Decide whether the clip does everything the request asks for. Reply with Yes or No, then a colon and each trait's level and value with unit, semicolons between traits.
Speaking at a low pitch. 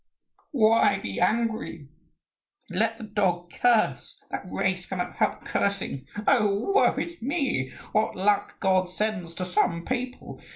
No: high, 210 Hz